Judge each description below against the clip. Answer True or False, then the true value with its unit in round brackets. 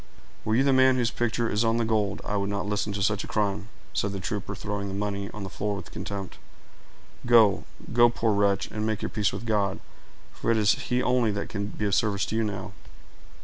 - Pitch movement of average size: False (2.1 semitones)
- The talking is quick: True (230 wpm)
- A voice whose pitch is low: True (105 Hz)